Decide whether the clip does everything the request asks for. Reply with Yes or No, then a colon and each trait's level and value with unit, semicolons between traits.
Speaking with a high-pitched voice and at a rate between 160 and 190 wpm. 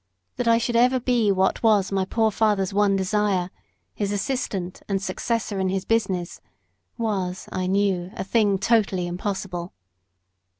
No: high, 200 Hz; average, 145 wpm